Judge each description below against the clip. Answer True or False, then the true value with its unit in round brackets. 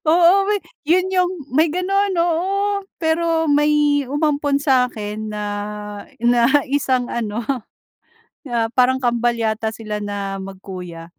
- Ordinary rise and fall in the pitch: False (7.0 semitones)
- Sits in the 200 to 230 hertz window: False (265 Hz)